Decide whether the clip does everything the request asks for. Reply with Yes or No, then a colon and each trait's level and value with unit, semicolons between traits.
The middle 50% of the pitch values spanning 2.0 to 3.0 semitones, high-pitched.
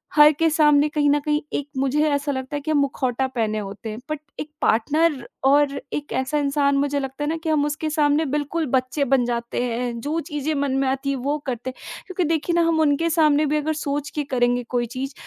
Yes: narrow, 2.4 semitones; very high, 285 Hz